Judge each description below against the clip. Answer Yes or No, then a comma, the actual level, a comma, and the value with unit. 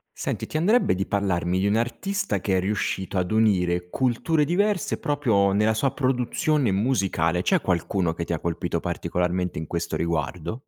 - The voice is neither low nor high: No, low, 100 Hz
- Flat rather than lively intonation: No, wide, 6.8 semitones